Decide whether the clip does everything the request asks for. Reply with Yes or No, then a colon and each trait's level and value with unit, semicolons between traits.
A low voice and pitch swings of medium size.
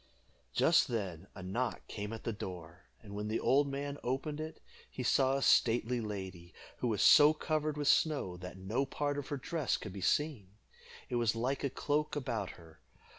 No: low, 120 Hz; wide, 6.5 semitones